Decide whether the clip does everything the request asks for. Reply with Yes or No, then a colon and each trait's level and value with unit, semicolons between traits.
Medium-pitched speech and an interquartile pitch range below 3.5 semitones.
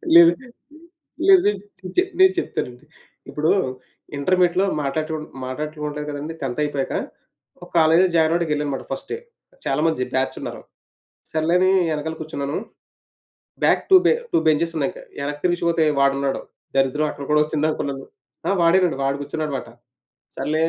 Yes: medium, 155 Hz; average, 2.9 semitones